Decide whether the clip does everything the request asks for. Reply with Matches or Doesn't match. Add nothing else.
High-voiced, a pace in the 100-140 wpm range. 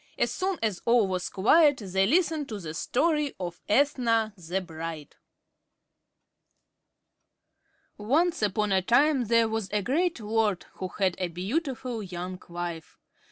Matches